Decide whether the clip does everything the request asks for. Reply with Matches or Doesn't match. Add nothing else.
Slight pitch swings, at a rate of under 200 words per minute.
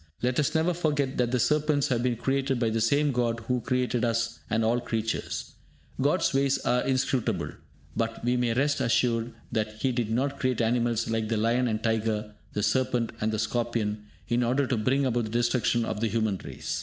Doesn't match